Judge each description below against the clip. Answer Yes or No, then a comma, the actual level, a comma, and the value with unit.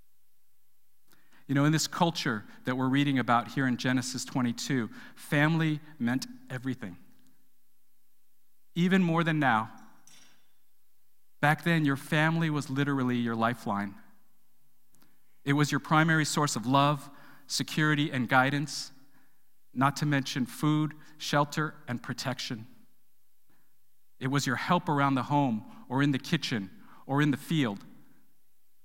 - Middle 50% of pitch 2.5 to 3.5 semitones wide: Yes, average, 3.0 semitones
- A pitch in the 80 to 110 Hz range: No, medium, 140 Hz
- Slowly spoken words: Yes, slow, 125 wpm